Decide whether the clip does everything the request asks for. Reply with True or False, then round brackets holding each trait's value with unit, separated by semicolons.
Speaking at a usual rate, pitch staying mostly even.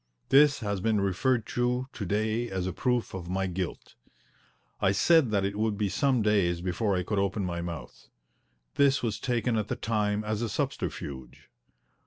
False (180 wpm; 3.7 semitones)